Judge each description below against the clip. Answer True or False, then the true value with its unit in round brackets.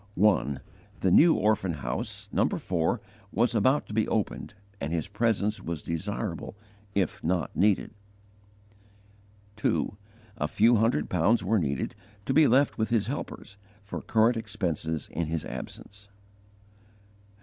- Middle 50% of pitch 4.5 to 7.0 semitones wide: True (5.1 semitones)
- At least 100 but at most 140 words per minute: True (135 wpm)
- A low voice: True (100 Hz)